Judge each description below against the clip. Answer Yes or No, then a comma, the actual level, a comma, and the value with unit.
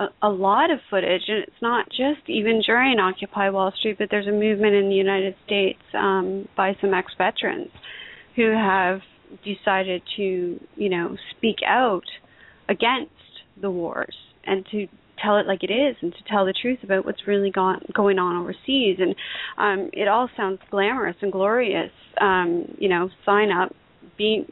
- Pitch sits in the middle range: No, high, 200 Hz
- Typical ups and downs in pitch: No, narrow, 2.1 semitones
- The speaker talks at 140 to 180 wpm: Yes, average, 170 wpm